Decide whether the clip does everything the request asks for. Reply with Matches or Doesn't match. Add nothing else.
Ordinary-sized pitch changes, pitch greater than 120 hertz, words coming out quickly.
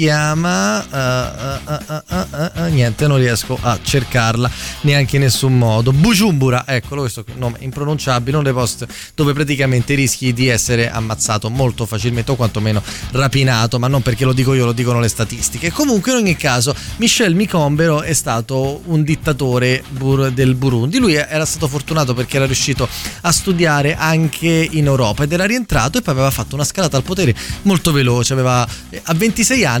Matches